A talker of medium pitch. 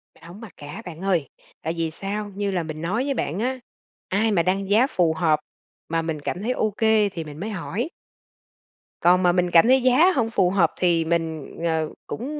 Yes: medium, 180 Hz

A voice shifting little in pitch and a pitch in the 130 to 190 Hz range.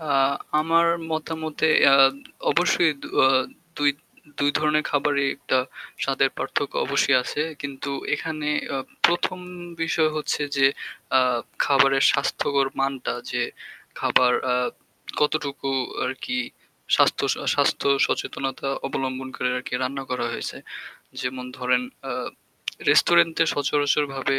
Yes: narrow, 2.2 semitones; medium, 140 Hz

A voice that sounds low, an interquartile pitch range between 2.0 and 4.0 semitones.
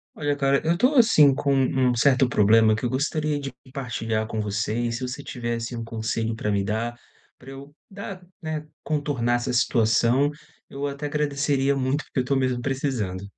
Yes: low, 130 Hz; average, 3.6 semitones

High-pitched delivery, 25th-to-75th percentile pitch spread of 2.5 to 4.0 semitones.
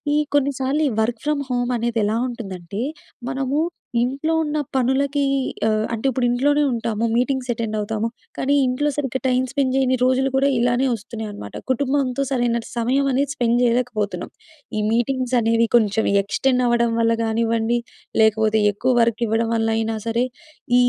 Yes: high, 240 Hz; average, 2.9 semitones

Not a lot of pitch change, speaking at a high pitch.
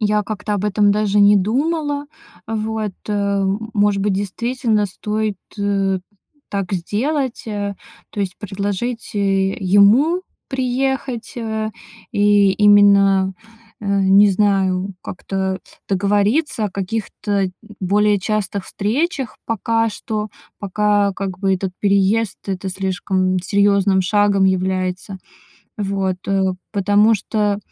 Yes: narrow, 1.8 semitones; high, 205 Hz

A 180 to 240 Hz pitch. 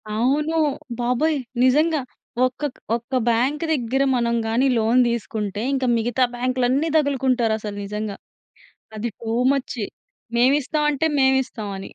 No: very high, 255 Hz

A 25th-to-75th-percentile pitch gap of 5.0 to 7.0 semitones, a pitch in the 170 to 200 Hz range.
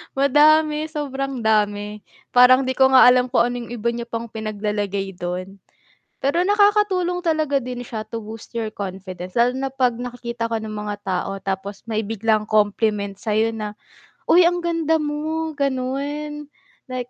No: wide, 5.5 semitones; high, 240 Hz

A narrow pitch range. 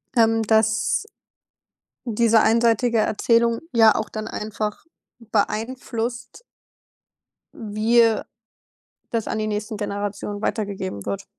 Yes: narrow, 1.7 semitones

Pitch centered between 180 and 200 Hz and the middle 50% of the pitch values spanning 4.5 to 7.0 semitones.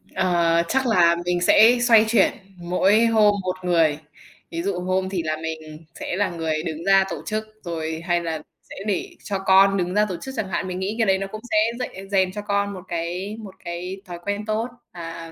No: medium, 185 Hz; average, 3.2 semitones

